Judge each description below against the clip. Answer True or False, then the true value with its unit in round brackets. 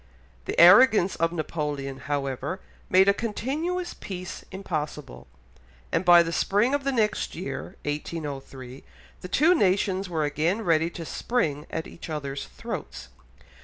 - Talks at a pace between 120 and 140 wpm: True (135 wpm)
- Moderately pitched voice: True (170 Hz)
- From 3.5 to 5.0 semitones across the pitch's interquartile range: False (5.4 semitones)